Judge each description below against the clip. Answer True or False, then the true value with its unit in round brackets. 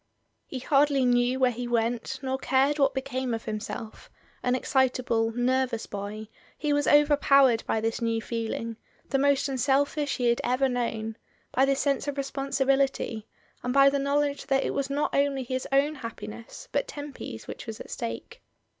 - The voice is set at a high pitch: True (260 Hz)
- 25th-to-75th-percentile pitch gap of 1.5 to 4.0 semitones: True (3.1 semitones)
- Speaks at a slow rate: False (170 wpm)